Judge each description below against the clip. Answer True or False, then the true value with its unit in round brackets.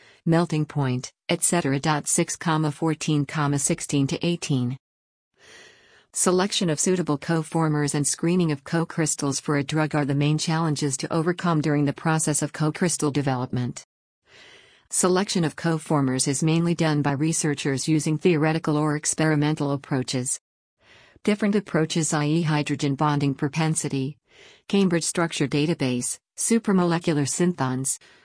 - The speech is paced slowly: True (120 wpm)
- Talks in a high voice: False (155 Hz)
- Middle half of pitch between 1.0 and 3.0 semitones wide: True (2.5 semitones)